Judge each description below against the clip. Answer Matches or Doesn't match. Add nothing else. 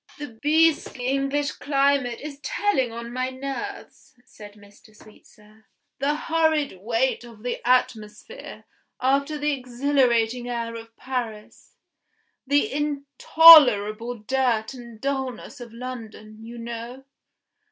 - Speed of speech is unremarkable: Doesn't match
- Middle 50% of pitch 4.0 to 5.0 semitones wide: Doesn't match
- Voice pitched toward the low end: Doesn't match